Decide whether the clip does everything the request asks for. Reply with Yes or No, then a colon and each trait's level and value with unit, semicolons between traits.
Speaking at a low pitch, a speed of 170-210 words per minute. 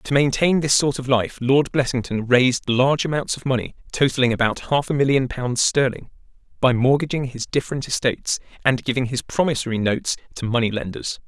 Yes: low, 130 Hz; average, 175 wpm